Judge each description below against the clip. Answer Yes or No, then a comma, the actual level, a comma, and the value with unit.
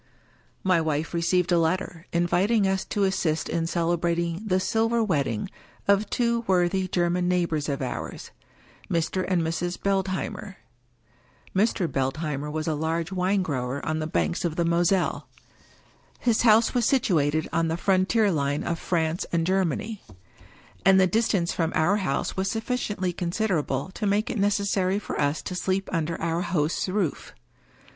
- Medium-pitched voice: Yes, medium, 175 Hz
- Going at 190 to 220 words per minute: No, average, 165 wpm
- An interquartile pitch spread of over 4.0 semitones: No, average, 3.2 semitones